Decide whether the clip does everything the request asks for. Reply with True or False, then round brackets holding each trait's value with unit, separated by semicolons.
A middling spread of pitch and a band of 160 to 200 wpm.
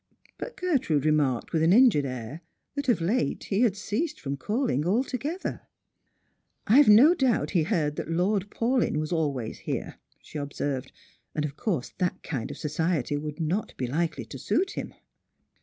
False (8.0 semitones; 175 wpm)